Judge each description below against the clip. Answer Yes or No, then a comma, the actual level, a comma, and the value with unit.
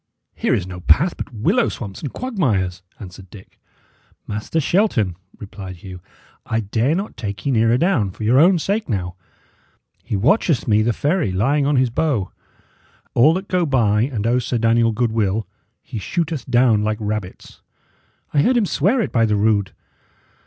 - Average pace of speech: Yes, average, 170 wpm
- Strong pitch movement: Yes, wide, 6.4 semitones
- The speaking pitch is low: Yes, low, 115 Hz